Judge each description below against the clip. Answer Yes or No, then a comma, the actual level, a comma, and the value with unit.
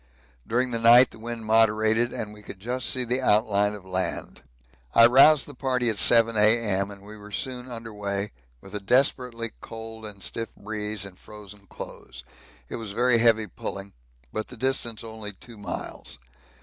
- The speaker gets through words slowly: No, average, 175 wpm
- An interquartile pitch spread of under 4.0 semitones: Yes, narrow, 2.5 semitones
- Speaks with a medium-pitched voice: No, low, 110 Hz